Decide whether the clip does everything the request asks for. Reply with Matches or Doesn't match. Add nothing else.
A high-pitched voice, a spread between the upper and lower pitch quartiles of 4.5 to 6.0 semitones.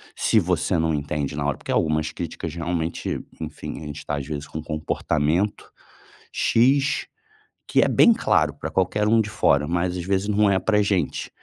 Doesn't match